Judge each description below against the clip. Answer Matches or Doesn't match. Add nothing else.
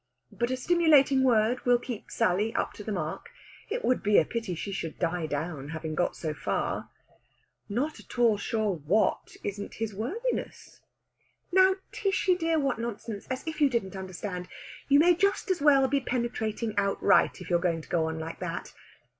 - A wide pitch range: Matches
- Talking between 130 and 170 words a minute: Doesn't match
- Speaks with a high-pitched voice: Matches